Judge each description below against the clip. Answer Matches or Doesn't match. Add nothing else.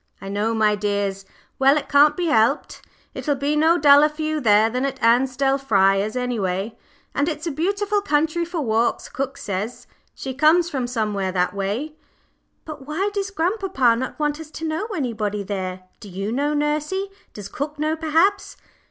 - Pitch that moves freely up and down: Matches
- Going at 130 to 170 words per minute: Doesn't match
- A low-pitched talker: Doesn't match